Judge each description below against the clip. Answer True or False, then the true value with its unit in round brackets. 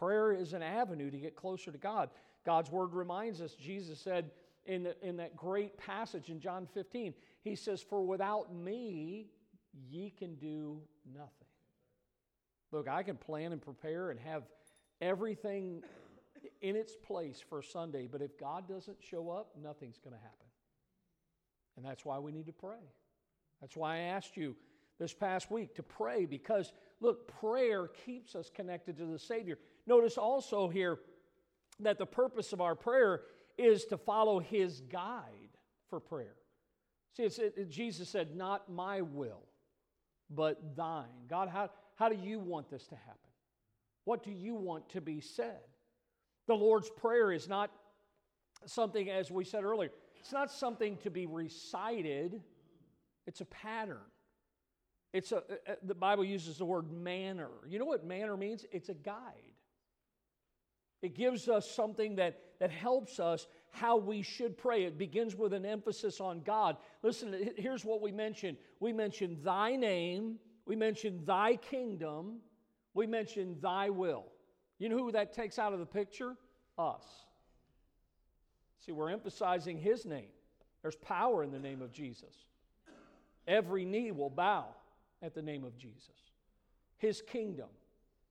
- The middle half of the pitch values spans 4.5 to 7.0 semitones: True (4.8 semitones)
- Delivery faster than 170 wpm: False (155 wpm)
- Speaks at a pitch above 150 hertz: True (190 Hz)